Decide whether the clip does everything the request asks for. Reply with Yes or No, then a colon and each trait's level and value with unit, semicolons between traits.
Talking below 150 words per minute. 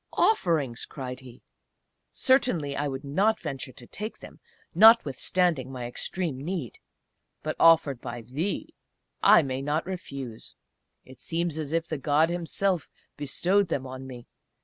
Yes: average, 140 wpm